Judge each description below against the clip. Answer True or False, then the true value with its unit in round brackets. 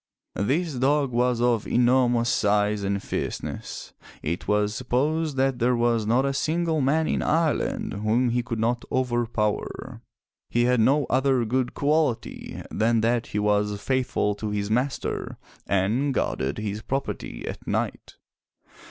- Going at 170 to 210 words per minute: False (145 wpm)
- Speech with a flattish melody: False (3.9 semitones)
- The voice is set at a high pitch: False (120 Hz)